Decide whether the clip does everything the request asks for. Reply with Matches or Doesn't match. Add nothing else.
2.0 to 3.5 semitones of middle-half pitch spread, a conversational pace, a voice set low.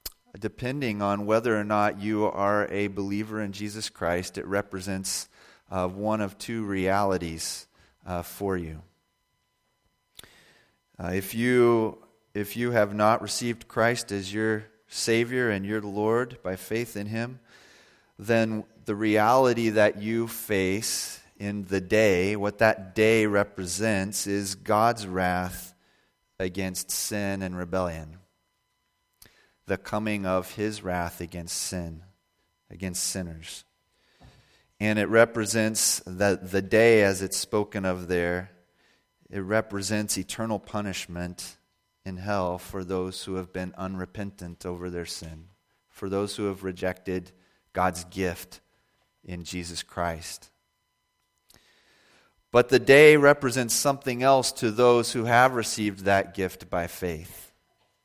Doesn't match